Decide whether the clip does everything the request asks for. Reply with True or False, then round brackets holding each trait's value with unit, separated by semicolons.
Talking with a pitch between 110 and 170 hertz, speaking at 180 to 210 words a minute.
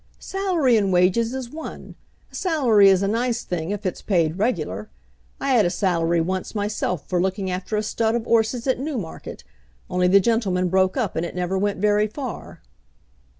False (205 Hz; 185 wpm)